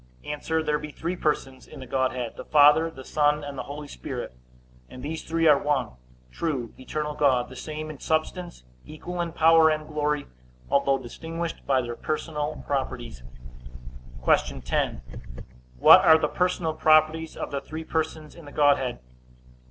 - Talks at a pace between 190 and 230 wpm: No, average, 160 wpm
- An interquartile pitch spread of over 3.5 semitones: No, average, 2.9 semitones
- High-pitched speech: No, medium, 150 Hz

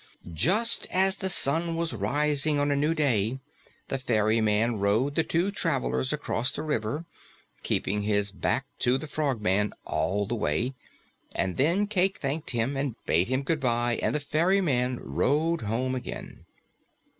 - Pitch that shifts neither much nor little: No, wide, 6.2 semitones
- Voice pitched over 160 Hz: No, low, 130 Hz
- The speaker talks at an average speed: Yes, average, 150 wpm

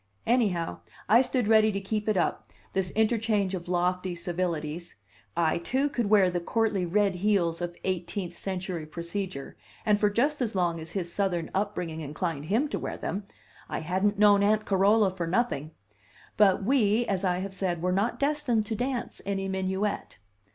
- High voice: Yes, high, 195 Hz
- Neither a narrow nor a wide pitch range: Yes, average, 3.4 semitones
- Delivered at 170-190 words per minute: Yes, average, 175 wpm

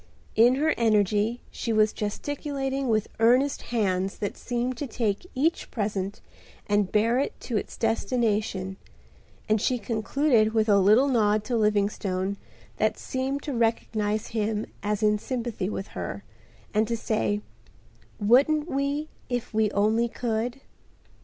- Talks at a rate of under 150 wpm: Yes, average, 140 wpm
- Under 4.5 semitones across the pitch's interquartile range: Yes, average, 3.2 semitones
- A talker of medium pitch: No, high, 220 Hz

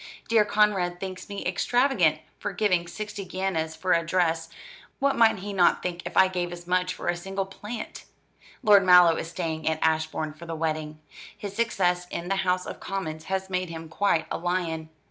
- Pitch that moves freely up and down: No, average, 2.9 semitones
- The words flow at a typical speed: Yes, average, 190 wpm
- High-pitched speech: No, medium, 180 Hz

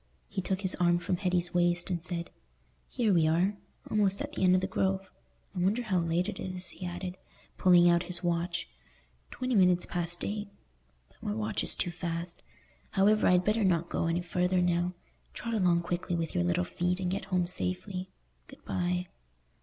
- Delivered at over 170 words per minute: Yes, average, 185 wpm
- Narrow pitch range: Yes, narrow, 1.6 semitones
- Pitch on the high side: No, medium, 180 Hz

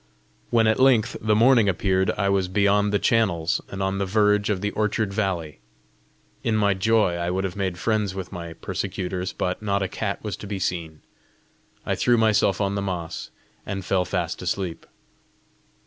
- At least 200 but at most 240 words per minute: No, average, 180 wpm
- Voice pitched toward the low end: Yes, low, 100 Hz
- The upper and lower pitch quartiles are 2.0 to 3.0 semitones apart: Yes, narrow, 2.4 semitones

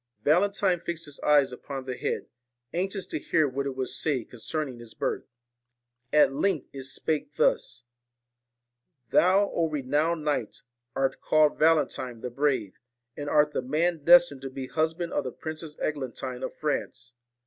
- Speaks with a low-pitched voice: No, medium, 150 Hz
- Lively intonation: No, average, 3.7 semitones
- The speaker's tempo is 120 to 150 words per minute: No, average, 160 wpm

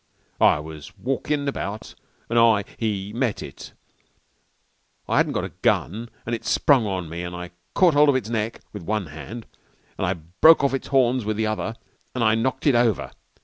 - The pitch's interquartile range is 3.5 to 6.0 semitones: Yes, average, 4.9 semitones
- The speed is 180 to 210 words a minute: Yes, average, 190 wpm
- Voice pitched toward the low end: Yes, low, 110 Hz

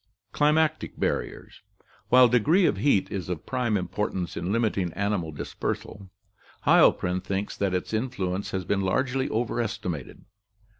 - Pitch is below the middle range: Yes, low, 100 Hz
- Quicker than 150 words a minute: No, slow, 135 wpm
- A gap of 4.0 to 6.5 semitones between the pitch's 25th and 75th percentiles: Yes, average, 5.3 semitones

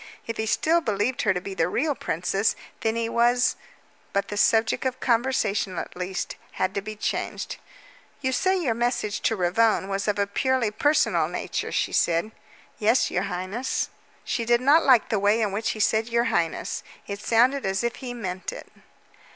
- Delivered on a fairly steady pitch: No, average, 3.5 semitones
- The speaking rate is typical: Yes, average, 185 wpm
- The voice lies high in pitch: Yes, high, 220 Hz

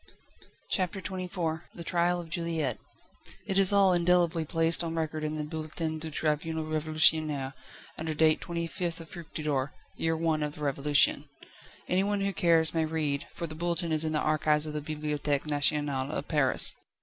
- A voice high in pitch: No, medium, 160 Hz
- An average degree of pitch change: No, narrow, 2.0 semitones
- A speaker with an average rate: Yes, average, 160 wpm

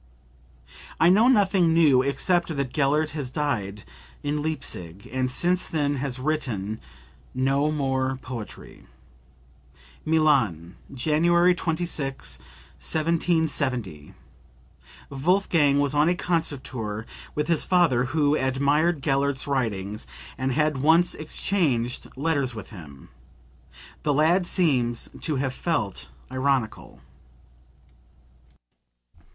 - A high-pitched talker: No, medium, 140 Hz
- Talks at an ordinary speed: No, slow, 100 wpm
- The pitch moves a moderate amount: Yes, average, 4.1 semitones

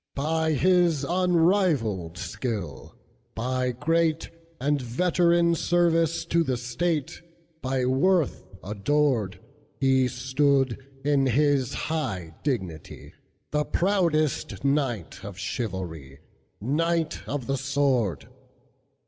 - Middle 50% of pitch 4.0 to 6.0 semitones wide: Yes, average, 5.2 semitones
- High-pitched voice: No, medium, 140 Hz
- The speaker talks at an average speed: No, slow, 80 wpm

